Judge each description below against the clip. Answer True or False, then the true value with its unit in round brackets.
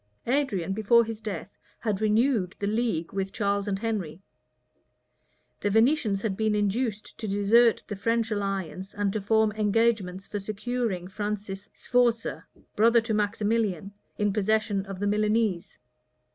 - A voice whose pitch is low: False (210 Hz)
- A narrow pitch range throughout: True (2.3 semitones)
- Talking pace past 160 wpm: False (145 wpm)